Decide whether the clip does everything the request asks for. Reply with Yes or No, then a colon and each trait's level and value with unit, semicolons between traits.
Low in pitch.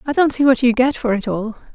No: very high, 250 Hz